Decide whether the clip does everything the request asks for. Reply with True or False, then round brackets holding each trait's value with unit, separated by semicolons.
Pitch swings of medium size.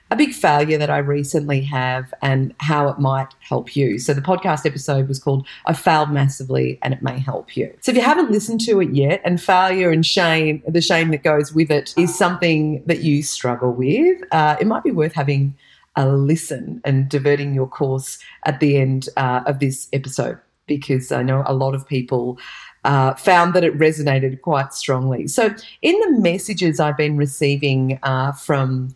True (3.5 semitones)